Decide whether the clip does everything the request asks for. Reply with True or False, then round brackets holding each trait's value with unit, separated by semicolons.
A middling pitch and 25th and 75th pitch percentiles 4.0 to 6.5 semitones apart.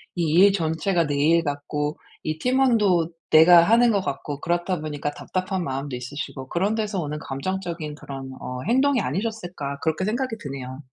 True (165 Hz; 5.2 semitones)